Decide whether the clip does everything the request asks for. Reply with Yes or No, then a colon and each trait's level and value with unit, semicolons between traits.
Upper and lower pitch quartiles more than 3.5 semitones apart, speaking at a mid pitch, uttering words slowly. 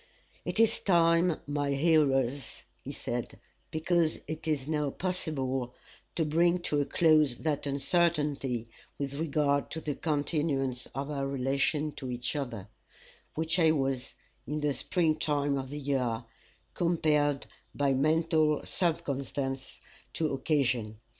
No: average, 2.8 semitones; medium, 145 Hz; slow, 130 wpm